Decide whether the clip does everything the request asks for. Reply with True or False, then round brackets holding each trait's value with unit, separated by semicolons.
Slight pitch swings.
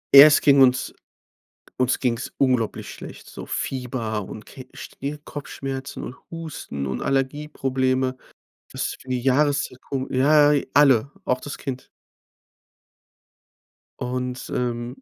True (1.9 semitones)